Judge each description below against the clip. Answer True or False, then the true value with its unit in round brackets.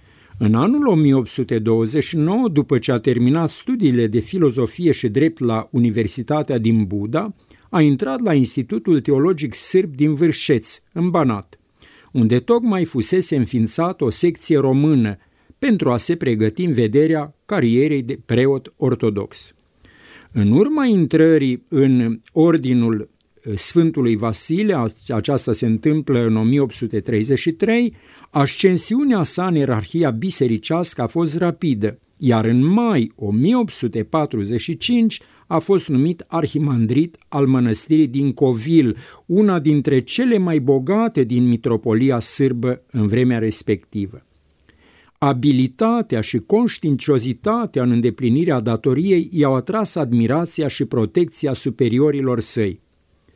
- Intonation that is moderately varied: False (5.9 semitones)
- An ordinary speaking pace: False (110 wpm)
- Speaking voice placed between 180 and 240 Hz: False (135 Hz)